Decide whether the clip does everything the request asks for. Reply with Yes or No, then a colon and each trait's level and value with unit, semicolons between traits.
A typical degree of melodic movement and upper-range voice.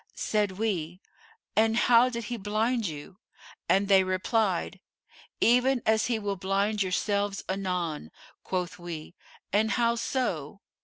Yes: average, 3.4 semitones; high, 200 Hz